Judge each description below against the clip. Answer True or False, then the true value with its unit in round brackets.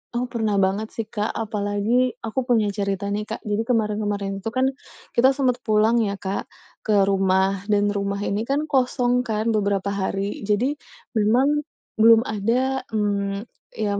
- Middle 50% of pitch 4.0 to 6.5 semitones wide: False (2.9 semitones)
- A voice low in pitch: False (210 Hz)